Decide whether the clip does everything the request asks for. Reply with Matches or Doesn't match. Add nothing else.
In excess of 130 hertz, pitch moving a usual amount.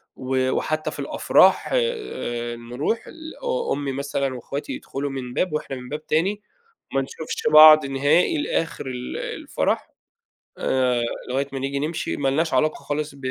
Matches